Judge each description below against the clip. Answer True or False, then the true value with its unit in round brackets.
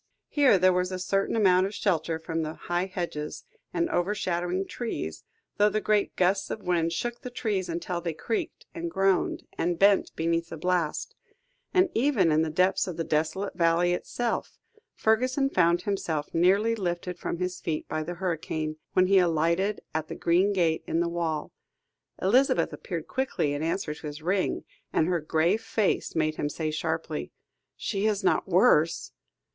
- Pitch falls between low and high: True (180 Hz)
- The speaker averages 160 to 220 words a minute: True (175 wpm)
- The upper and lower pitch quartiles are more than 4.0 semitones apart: False (3.5 semitones)